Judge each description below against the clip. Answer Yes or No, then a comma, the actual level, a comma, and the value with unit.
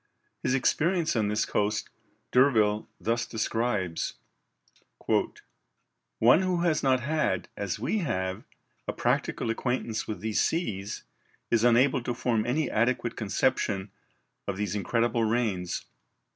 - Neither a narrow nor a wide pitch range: Yes, average, 3.6 semitones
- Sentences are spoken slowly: Yes, slow, 120 wpm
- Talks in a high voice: No, low, 115 Hz